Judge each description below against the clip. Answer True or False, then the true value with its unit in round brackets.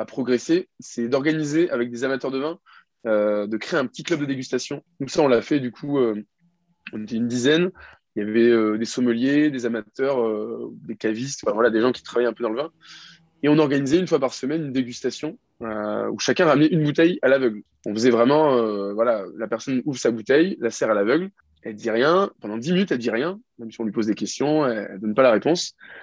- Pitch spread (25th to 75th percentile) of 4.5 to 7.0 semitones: True (5.3 semitones)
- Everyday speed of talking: False (235 wpm)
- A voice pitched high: False (125 Hz)